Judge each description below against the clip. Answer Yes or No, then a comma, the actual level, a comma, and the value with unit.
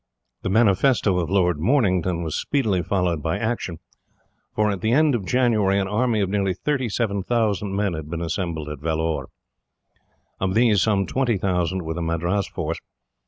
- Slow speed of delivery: No, average, 160 wpm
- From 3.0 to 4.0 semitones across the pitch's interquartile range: No, average, 4.4 semitones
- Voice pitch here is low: Yes, very low, 95 Hz